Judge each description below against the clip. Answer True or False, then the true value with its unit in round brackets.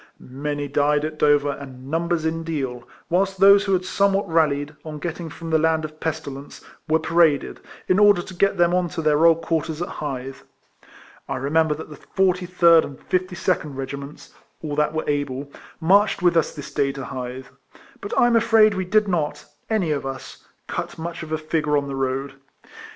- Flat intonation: False (3.6 semitones)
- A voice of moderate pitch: True (160 Hz)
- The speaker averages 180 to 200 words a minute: True (190 wpm)